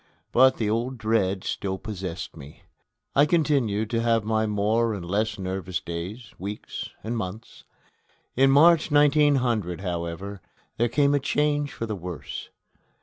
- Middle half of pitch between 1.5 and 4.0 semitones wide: No, wide, 5.6 semitones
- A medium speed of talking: Yes, average, 145 wpm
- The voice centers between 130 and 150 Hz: No, low, 110 Hz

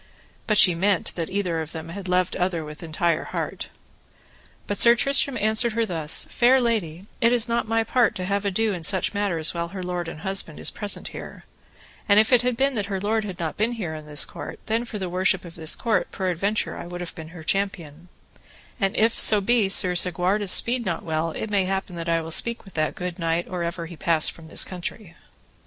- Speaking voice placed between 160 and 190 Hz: Yes, medium, 185 Hz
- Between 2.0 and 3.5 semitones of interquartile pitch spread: No, average, 4.3 semitones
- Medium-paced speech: No, fast, 225 wpm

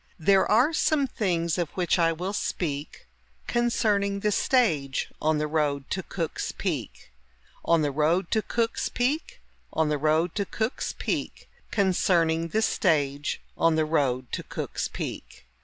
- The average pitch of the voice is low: No, medium, 170 Hz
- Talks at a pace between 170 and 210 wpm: No, average, 150 wpm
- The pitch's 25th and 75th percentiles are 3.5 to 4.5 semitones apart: No, average, 5.1 semitones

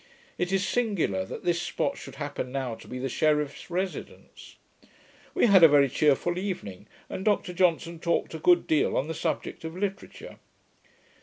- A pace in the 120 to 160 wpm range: No, average, 170 wpm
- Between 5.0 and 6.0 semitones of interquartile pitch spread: No, average, 4.6 semitones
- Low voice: No, medium, 170 Hz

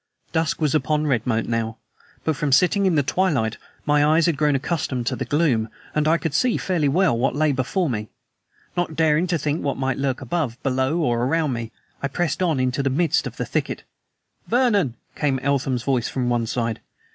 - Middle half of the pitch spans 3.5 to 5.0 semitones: Yes, average, 4.1 semitones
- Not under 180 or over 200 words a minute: Yes, average, 190 wpm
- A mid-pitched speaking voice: Yes, medium, 145 Hz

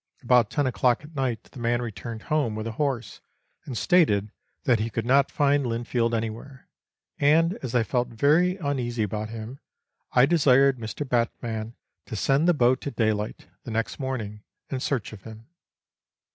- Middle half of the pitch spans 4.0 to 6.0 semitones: No, average, 3.6 semitones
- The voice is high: No, low, 120 Hz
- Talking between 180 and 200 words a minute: No, average, 170 wpm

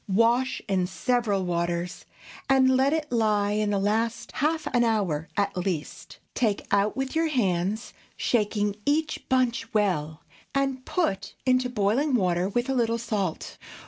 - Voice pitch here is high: Yes, high, 220 Hz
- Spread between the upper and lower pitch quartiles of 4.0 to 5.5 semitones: Yes, average, 4.7 semitones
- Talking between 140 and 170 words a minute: Yes, average, 145 wpm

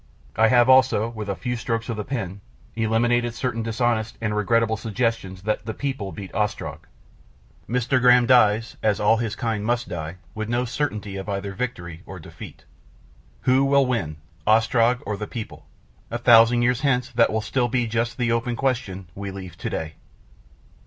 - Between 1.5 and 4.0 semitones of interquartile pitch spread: Yes, average, 2.7 semitones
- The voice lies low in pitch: Yes, low, 115 Hz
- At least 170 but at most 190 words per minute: Yes, average, 175 wpm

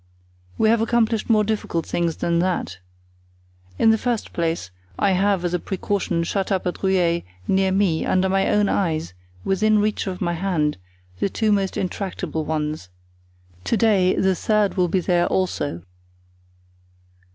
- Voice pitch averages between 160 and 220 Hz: Yes, high, 190 Hz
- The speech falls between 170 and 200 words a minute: No, average, 155 wpm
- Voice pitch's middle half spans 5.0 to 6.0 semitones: No, average, 3.2 semitones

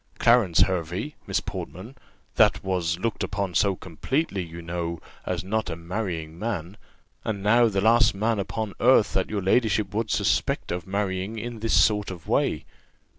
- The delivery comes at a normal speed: Yes, average, 165 wpm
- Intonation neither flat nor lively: Yes, average, 3.8 semitones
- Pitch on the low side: Yes, low, 100 Hz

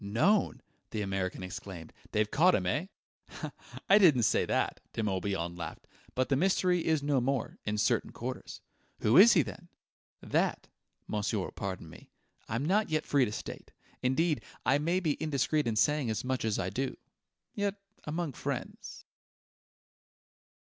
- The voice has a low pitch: Yes, low, 130 Hz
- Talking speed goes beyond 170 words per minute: No, average, 155 wpm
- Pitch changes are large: Yes, wide, 7.3 semitones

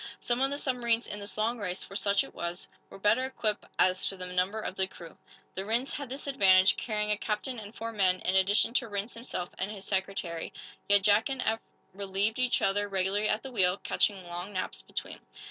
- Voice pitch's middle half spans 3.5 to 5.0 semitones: No, average, 3.1 semitones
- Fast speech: Yes, fast, 215 wpm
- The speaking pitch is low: No, high, 205 Hz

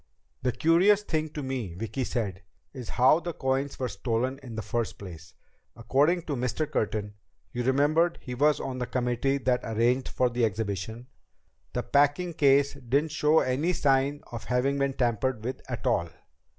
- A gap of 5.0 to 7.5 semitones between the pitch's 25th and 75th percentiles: No, average, 3.5 semitones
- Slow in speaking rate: No, average, 170 wpm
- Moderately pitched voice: No, low, 130 Hz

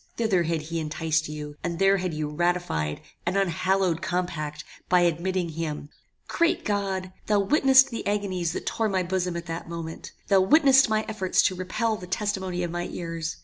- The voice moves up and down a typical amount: Yes, average, 3.1 semitones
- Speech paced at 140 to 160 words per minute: No, average, 180 wpm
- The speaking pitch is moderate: Yes, medium, 180 Hz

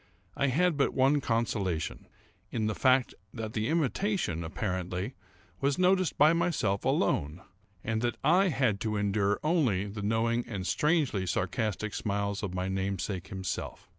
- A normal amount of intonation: No, wide, 6.1 semitones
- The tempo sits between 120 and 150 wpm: Yes, average, 140 wpm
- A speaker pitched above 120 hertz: No, low, 110 Hz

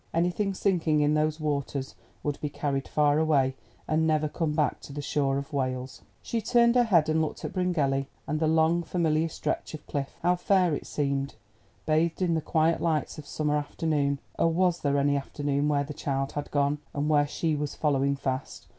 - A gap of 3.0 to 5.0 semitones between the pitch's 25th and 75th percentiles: No, narrow, 2.4 semitones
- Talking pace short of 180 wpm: No, average, 200 wpm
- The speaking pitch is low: No, medium, 150 Hz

